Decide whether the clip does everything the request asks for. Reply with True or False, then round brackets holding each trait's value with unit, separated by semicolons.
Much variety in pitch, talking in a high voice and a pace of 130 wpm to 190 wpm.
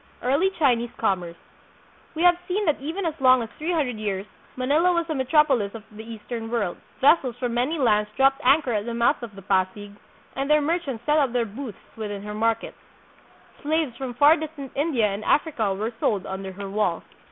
False (5.9 semitones; 245 Hz; 200 wpm)